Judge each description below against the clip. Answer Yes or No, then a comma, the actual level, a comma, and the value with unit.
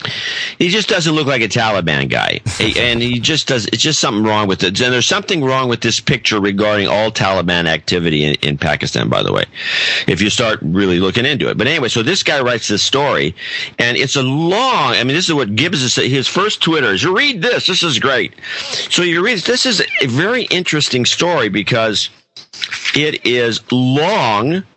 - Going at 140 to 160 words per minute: No, fast, 205 wpm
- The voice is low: Yes, low, 120 Hz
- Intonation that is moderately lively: No, wide, 7.3 semitones